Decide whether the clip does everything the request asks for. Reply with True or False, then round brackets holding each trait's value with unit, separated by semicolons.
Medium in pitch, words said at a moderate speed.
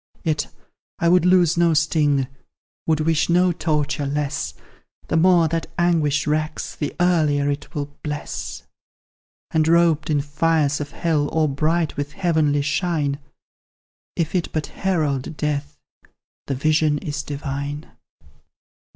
False (155 Hz; 130 wpm)